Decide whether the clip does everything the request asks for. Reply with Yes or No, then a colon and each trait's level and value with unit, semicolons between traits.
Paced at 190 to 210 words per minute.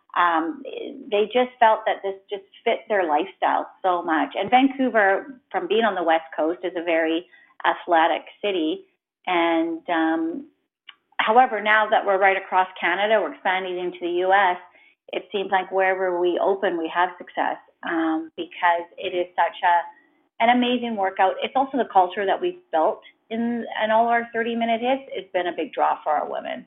No: average, 180 wpm